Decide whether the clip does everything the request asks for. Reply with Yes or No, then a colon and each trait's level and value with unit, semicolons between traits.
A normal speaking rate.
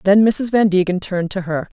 No: fast, 235 wpm